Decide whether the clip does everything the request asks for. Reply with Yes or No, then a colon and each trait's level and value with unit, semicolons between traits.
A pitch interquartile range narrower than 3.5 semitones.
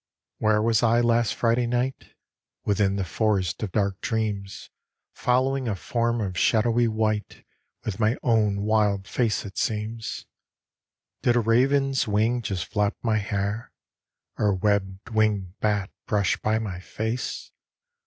Yes: narrow, 2.4 semitones